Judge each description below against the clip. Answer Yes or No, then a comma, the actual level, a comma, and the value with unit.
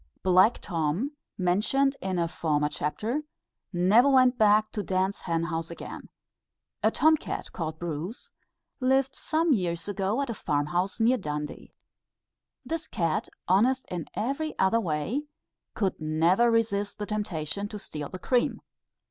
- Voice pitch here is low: No, high, 195 Hz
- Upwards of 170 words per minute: No, average, 145 wpm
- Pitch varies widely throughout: Yes, wide, 6.1 semitones